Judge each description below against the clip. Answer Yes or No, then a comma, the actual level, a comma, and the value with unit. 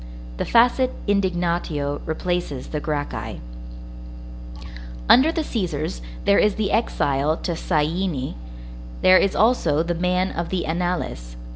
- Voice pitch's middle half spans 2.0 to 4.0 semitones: No, average, 4.6 semitones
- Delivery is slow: Yes, slow, 120 wpm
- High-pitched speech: No, medium, 175 Hz